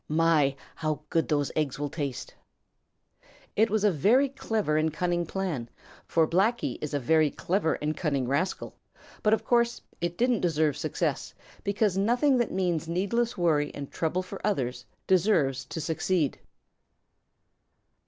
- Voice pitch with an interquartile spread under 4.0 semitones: No, average, 5.2 semitones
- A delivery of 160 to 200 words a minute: No, average, 145 wpm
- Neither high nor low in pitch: Yes, medium, 170 Hz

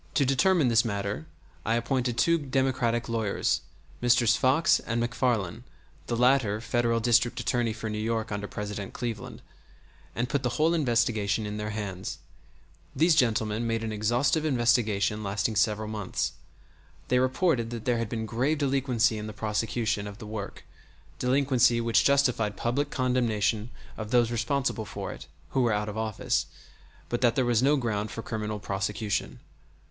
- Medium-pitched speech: No, low, 115 Hz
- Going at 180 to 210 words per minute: No, average, 160 wpm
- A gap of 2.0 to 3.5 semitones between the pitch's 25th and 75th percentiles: Yes, average, 2.9 semitones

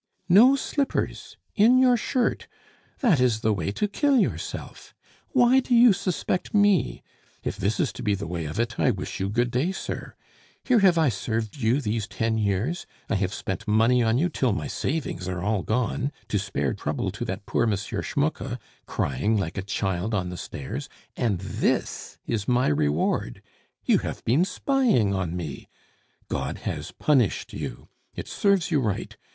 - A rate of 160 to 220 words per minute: Yes, average, 175 wpm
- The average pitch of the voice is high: No, low, 115 Hz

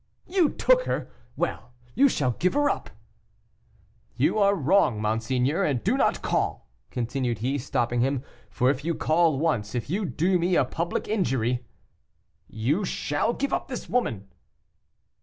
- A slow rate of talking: No, average, 160 wpm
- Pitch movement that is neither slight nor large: No, wide, 7.8 semitones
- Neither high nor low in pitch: Yes, medium, 145 Hz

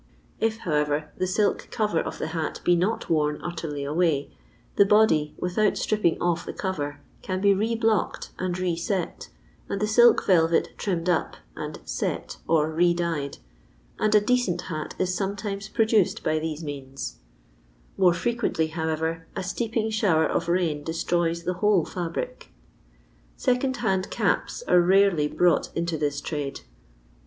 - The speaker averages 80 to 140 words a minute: No, average, 155 wpm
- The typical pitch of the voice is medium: Yes, medium, 175 Hz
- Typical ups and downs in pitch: Yes, average, 4.2 semitones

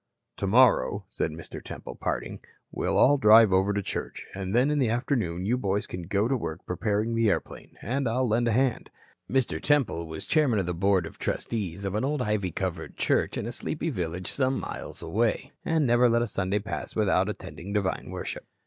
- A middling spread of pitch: Yes, average, 4.5 semitones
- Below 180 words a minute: No, average, 200 wpm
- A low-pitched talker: Yes, low, 105 Hz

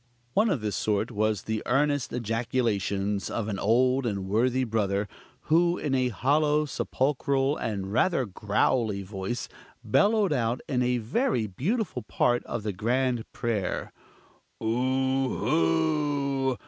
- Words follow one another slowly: Yes, slow, 125 wpm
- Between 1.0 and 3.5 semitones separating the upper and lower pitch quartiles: No, average, 4.3 semitones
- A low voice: Yes, low, 120 Hz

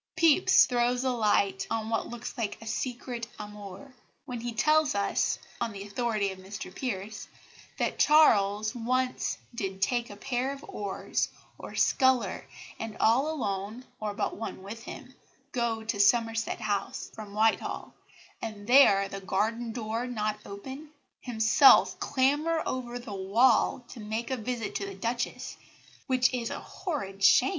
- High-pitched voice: Yes, high, 225 Hz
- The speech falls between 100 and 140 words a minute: No, average, 155 wpm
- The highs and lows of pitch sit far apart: No, average, 3.6 semitones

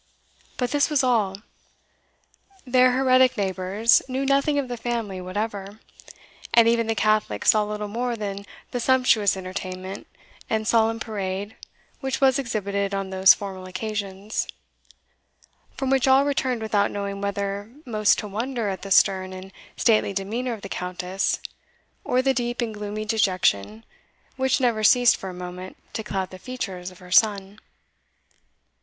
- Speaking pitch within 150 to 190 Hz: No, high, 210 Hz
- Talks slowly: No, average, 150 wpm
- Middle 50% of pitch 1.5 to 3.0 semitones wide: No, average, 3.9 semitones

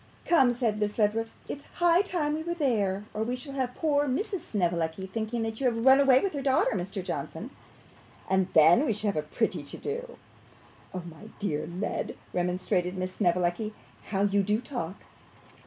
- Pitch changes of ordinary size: No, wide, 6.5 semitones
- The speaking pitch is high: Yes, high, 215 Hz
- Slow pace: No, average, 180 wpm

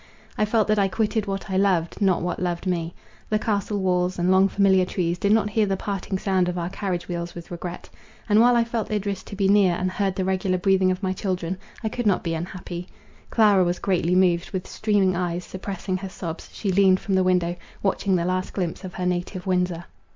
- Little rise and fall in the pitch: Yes, narrow, 1.9 semitones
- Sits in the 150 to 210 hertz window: Yes, medium, 185 Hz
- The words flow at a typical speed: No, fast, 225 wpm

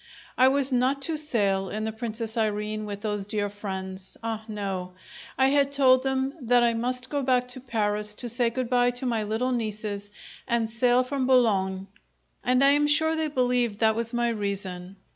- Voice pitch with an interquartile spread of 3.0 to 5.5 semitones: Yes, average, 3.5 semitones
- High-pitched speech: Yes, high, 235 Hz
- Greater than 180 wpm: Yes, average, 190 wpm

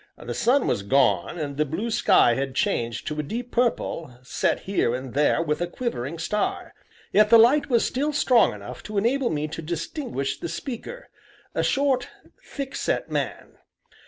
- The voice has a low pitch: No, medium, 170 Hz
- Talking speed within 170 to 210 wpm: Yes, average, 175 wpm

